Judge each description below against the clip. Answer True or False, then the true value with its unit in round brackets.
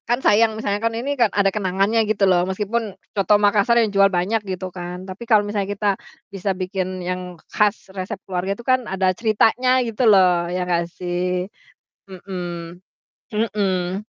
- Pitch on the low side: False (195 Hz)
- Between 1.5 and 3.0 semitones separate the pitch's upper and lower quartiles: True (2.7 semitones)